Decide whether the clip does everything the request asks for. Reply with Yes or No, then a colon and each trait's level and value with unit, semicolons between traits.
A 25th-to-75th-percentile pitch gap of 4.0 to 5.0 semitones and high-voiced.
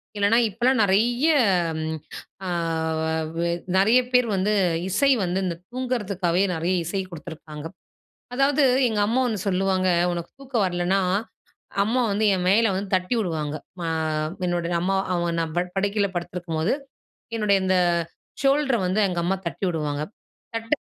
Yes: average, 4.5 semitones; high, 195 Hz